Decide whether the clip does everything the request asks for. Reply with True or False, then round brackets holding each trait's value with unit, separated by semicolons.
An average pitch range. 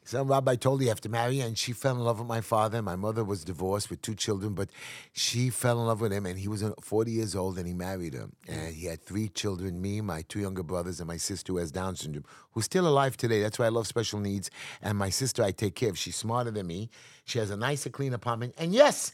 True (4.1 semitones)